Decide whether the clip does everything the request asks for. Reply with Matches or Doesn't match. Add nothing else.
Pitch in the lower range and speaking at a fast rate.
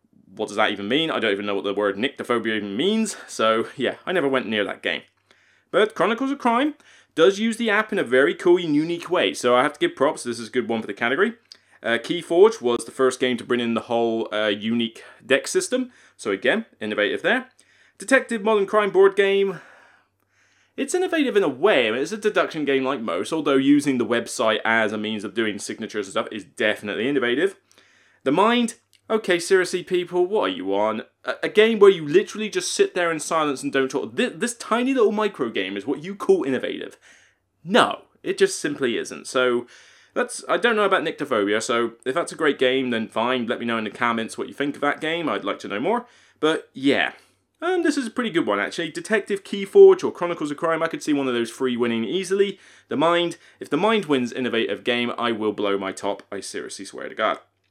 Doesn't match